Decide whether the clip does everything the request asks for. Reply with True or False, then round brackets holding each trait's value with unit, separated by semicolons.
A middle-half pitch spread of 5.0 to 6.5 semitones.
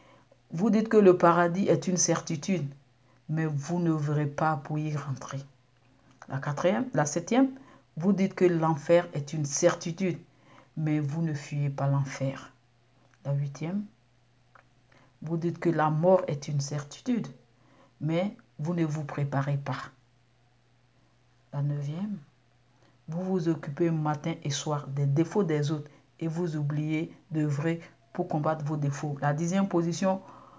False (3.6 semitones)